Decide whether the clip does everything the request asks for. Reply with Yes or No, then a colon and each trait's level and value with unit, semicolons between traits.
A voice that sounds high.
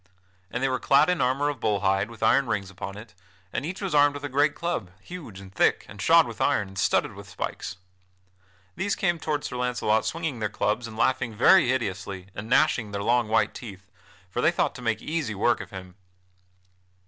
No: low, 120 Hz